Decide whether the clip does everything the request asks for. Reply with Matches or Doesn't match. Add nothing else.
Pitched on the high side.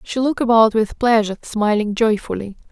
Matches